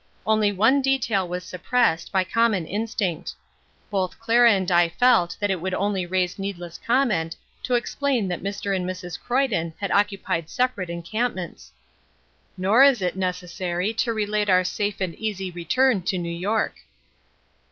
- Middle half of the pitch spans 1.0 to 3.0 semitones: No, average, 4.0 semitones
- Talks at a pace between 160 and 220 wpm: No, average, 150 wpm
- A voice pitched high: Yes, high, 195 Hz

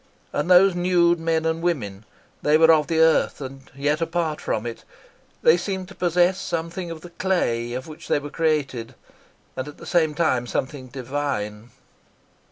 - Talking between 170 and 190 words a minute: Yes, average, 175 wpm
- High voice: No, medium, 160 Hz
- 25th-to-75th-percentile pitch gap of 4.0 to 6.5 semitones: Yes, average, 4.4 semitones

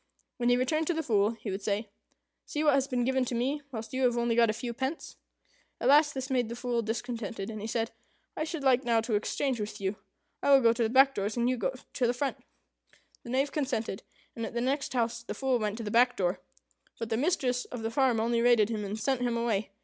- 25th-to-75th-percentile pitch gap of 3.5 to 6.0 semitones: No, average, 2.8 semitones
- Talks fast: Yes, fast, 250 wpm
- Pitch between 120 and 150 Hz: No, high, 240 Hz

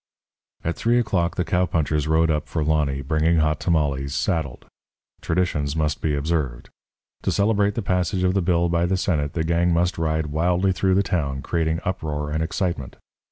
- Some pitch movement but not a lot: Yes, average, 3.0 semitones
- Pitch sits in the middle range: No, very low, 80 Hz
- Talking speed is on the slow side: No, average, 175 wpm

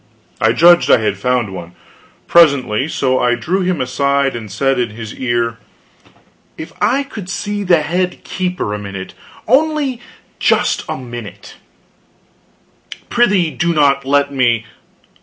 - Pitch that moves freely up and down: Yes, wide, 7.1 semitones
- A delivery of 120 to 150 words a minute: Yes, average, 140 wpm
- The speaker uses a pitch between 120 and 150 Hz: Yes, medium, 140 Hz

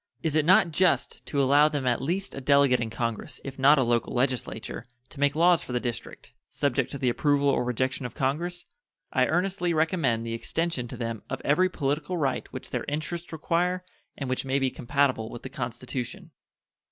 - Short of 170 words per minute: No, average, 195 wpm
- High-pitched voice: No, medium, 140 Hz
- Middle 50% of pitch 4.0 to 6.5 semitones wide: Yes, average, 4.6 semitones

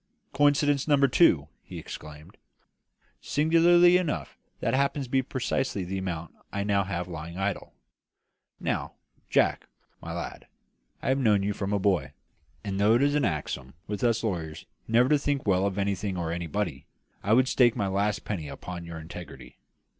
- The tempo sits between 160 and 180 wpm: Yes, average, 170 wpm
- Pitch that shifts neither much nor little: No, wide, 7.1 semitones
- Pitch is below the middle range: Yes, low, 100 Hz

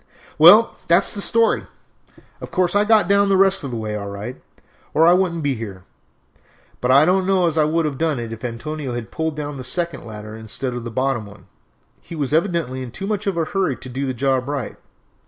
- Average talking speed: No, fast, 235 wpm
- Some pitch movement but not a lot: No, wide, 6.4 semitones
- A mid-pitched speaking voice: Yes, medium, 145 Hz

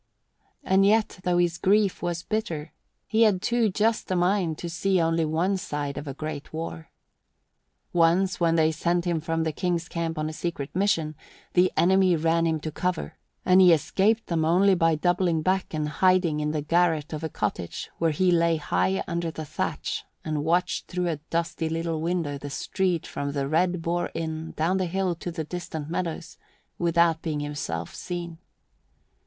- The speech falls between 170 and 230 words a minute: Yes, average, 180 wpm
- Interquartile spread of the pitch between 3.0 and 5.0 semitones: No, narrow, 2.4 semitones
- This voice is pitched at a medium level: Yes, medium, 170 Hz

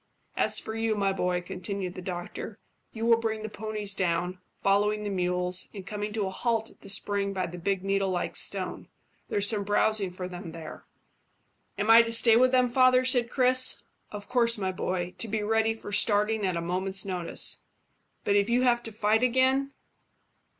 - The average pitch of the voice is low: No, high, 205 Hz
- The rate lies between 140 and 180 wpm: No, average, 190 wpm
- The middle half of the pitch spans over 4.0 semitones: No, average, 3.3 semitones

